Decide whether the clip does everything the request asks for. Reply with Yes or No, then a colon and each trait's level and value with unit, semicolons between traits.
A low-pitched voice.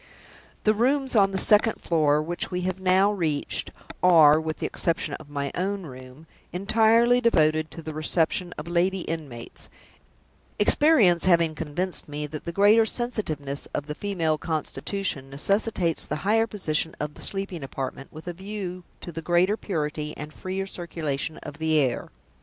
No: medium, 170 Hz